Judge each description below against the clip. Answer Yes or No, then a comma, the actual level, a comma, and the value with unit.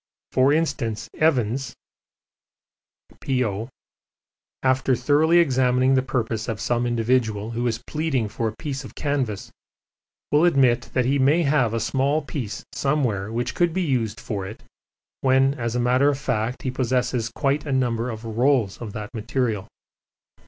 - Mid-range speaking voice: No, low, 125 Hz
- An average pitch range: Yes, average, 3.3 semitones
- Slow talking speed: No, average, 150 wpm